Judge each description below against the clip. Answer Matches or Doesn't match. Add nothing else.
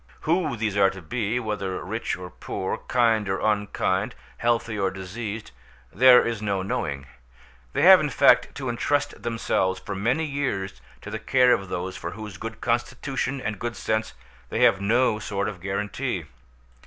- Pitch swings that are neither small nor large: Matches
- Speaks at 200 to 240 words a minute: Doesn't match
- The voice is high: Doesn't match